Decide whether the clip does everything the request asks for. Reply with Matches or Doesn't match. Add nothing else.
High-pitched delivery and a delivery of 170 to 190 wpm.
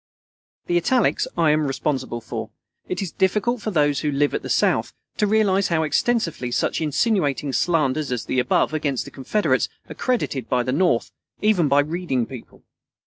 Doesn't match